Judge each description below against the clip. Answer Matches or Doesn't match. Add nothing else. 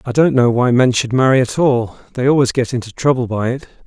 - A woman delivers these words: Doesn't match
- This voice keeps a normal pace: Doesn't match